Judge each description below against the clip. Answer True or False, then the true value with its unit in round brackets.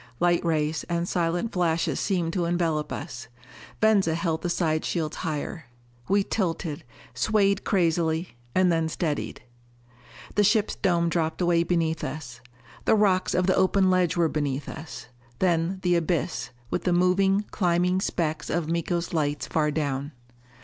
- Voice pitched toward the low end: False (170 Hz)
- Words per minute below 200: True (150 wpm)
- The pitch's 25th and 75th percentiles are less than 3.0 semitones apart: True (2.5 semitones)